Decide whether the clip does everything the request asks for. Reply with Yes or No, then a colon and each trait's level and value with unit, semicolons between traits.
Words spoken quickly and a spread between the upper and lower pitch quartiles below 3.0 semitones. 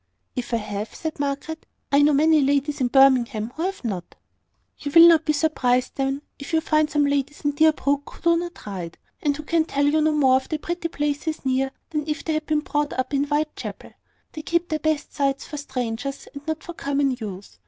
Yes: fast, 215 wpm; narrow, 2.5 semitones